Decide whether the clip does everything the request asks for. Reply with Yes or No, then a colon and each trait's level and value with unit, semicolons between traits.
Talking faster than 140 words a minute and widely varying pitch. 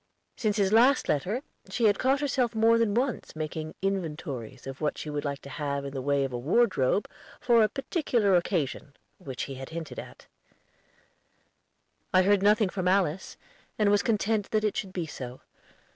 Yes: average, 180 wpm; wide, 7.2 semitones